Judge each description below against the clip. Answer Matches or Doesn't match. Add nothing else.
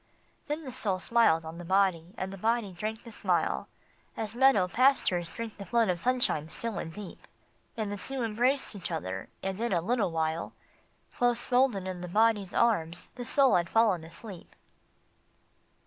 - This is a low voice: Doesn't match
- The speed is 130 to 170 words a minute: Doesn't match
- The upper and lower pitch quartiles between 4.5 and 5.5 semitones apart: Matches